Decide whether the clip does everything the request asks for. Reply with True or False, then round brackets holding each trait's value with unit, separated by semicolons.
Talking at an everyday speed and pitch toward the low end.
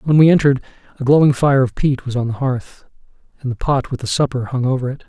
False (250 wpm; 130 Hz)